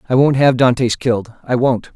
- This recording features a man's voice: Yes, male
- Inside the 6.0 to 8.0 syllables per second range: No, 5.3 syllables/s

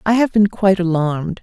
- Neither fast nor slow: No, fast, 210 wpm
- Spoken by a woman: Yes, female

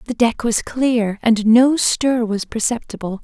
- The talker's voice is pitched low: No, high, 230 Hz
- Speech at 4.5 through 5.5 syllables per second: No, 4.0 syllables/s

